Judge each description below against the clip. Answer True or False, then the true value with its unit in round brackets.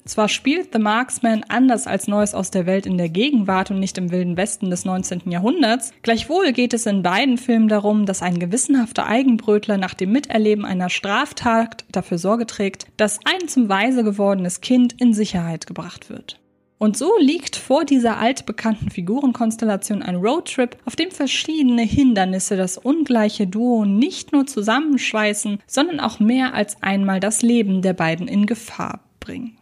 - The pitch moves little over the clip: False (4.3 semitones)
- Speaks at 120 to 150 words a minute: False (165 wpm)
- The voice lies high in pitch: True (215 Hz)